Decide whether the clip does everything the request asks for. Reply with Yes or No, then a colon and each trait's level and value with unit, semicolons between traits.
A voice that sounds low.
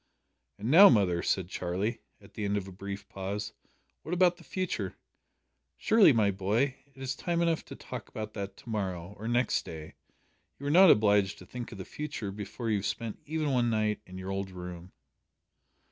Yes: low, 105 Hz